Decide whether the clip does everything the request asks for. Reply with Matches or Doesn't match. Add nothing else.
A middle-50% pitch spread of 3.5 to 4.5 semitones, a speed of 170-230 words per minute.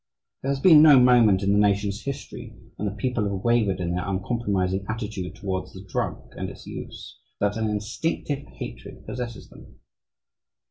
Matches